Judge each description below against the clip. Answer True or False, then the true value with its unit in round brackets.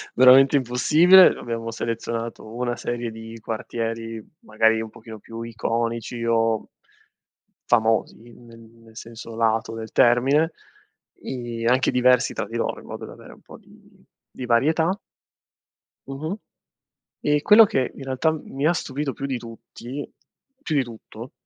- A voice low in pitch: True (120 Hz)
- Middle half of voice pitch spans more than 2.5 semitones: True (2.9 semitones)